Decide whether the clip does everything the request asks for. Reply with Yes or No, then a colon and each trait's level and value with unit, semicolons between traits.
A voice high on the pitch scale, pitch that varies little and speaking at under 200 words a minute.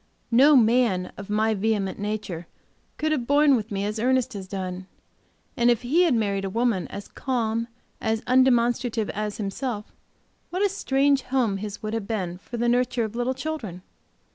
No: high, 225 Hz; average, 3.9 semitones; average, 175 wpm